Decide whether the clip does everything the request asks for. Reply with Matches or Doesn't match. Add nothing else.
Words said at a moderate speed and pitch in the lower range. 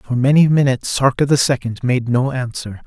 Matches